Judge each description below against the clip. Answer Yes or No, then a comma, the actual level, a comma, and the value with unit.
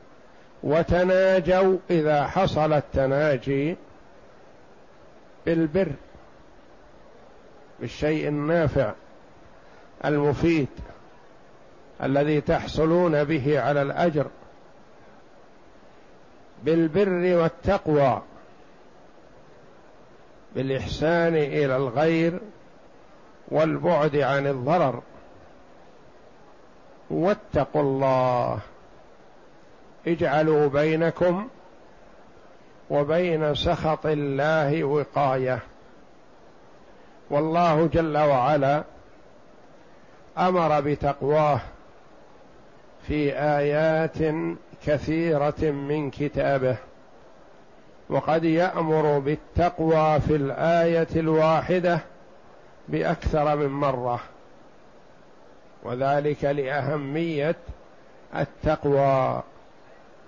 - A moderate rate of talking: No, slow, 50 wpm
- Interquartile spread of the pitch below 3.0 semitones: Yes, narrow, 2.5 semitones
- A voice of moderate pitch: Yes, medium, 150 Hz